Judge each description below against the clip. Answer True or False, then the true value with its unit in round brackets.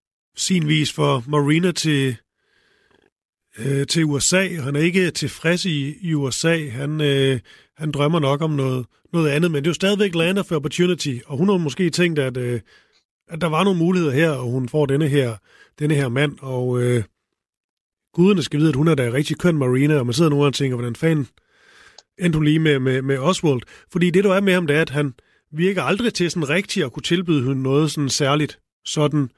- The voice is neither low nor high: True (150 Hz)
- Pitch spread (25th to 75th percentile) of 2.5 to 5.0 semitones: True (3.7 semitones)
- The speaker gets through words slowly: False (210 wpm)